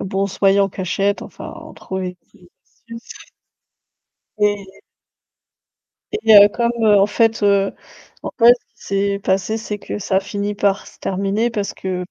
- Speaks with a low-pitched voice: No, high, 200 Hz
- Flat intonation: Yes, narrow, 1.3 semitones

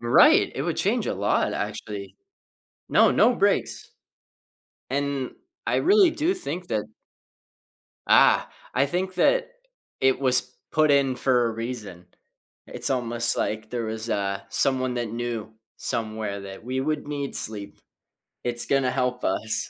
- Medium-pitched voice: No, low, 125 Hz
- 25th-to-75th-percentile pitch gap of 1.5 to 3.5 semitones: No, average, 4.1 semitones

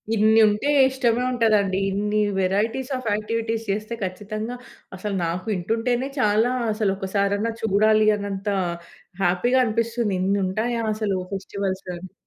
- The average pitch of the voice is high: Yes, high, 210 Hz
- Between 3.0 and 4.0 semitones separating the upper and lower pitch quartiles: No, narrow, 2.6 semitones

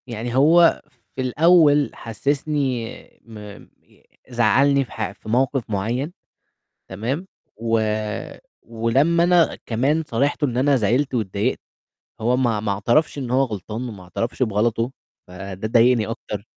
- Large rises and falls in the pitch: No, average, 4.1 semitones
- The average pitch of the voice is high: No, low, 120 Hz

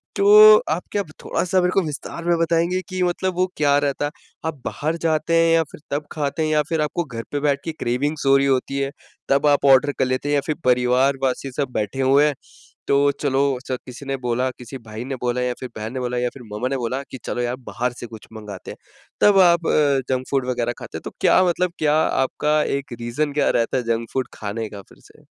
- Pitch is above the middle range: No, medium, 140 Hz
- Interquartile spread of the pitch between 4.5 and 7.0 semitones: No, average, 3.8 semitones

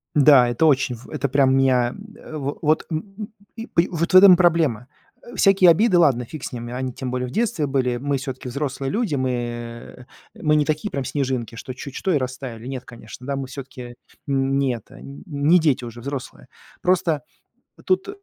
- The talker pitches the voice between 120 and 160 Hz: Yes, medium, 140 Hz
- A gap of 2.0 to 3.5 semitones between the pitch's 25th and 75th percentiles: No, average, 4.3 semitones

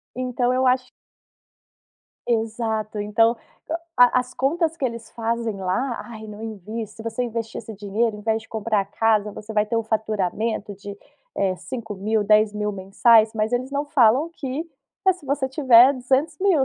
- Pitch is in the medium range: No, high, 225 Hz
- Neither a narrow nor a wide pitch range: Yes, average, 3.0 semitones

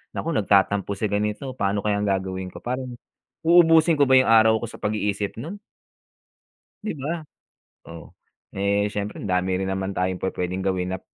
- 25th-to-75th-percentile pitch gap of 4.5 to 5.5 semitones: Yes, average, 5.1 semitones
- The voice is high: No, low, 105 Hz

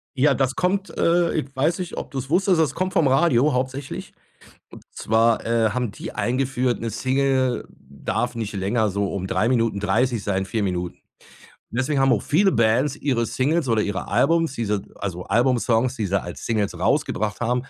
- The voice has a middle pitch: No, low, 125 Hz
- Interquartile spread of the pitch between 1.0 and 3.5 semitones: No, average, 4.1 semitones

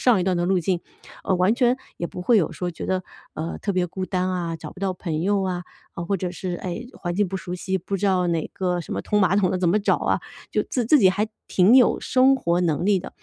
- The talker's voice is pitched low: No, medium, 185 Hz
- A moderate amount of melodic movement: No, narrow, 2.3 semitones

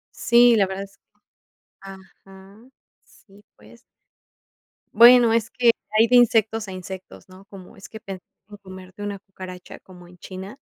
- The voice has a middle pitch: No, high, 195 Hz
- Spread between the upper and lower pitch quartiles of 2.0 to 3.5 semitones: Yes, average, 2.9 semitones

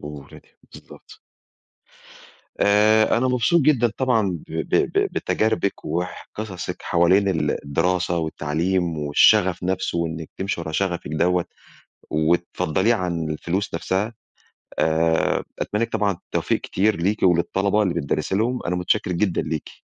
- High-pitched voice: No, very low, 90 Hz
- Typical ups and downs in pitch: Yes, average, 4.2 semitones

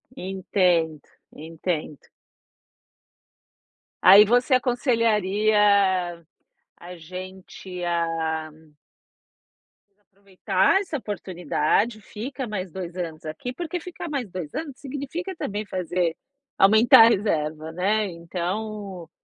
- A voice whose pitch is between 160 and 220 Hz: Yes, high, 190 Hz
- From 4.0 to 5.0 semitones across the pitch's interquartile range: Yes, average, 4.3 semitones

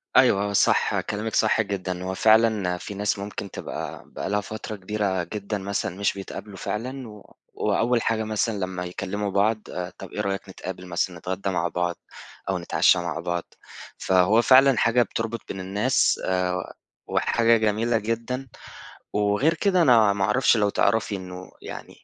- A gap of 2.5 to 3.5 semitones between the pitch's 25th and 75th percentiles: Yes, average, 3.2 semitones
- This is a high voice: No, low, 100 Hz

